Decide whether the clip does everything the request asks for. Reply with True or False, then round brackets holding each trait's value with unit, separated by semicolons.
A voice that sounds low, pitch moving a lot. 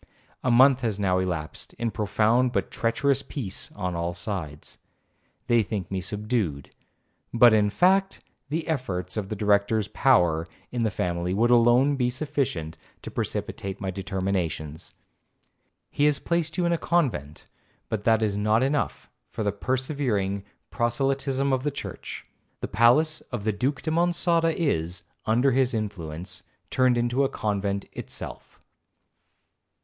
True (115 Hz; 5.7 semitones)